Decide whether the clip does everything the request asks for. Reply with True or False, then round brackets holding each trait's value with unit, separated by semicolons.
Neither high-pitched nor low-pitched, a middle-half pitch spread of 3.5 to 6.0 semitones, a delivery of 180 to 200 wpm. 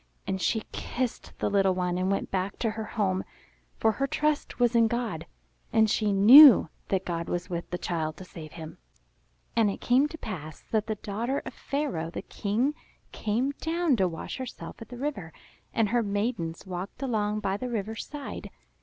False (210 Hz; 4.7 semitones; 190 wpm)